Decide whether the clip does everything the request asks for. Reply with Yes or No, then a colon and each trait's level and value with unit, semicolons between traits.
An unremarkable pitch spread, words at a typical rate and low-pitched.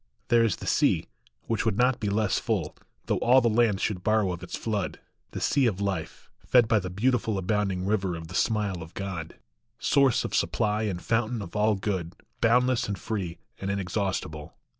Yes: average, 3.3 semitones; average, 190 wpm; low, 105 Hz